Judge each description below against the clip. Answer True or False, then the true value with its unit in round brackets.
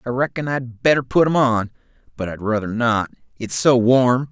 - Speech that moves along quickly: False (195 wpm)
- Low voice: True (125 Hz)